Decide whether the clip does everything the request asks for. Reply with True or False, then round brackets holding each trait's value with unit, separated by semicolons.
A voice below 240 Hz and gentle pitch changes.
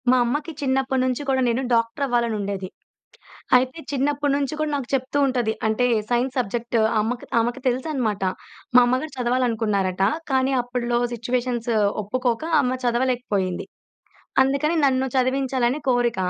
False (250 Hz; 2.0 semitones)